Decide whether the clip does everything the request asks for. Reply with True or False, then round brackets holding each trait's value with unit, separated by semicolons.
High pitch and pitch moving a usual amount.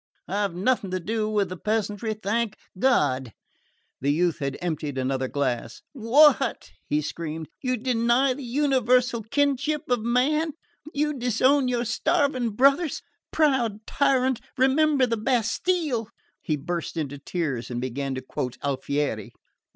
False (225 Hz; 8.9 semitones)